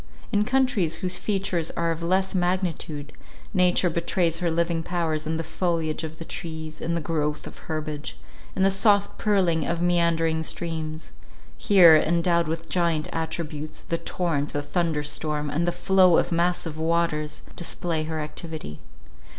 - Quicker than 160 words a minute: No, average, 155 wpm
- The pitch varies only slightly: Yes, narrow, 2.0 semitones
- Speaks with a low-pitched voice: No, medium, 165 Hz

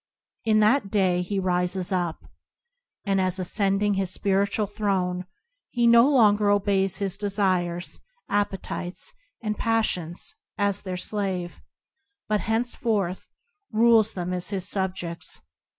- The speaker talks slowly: Yes, slow, 120 wpm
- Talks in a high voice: Yes, high, 195 Hz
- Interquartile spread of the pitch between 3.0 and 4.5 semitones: No, narrow, 2.4 semitones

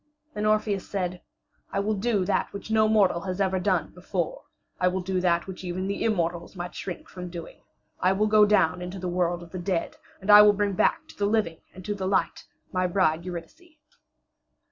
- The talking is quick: Yes, fast, 210 wpm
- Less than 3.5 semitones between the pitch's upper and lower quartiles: Yes, narrow, 2.5 semitones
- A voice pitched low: No, medium, 185 Hz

